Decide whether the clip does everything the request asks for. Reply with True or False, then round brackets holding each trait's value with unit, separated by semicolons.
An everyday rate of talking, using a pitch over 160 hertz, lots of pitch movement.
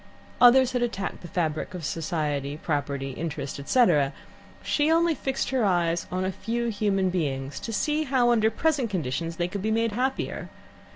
True (170 wpm; 190 Hz; 7.3 semitones)